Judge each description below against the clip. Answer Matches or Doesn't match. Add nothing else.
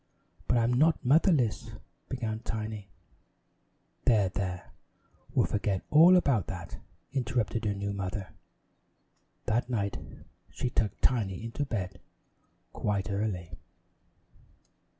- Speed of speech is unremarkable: Doesn't match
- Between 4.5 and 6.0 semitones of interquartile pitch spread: Doesn't match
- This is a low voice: Matches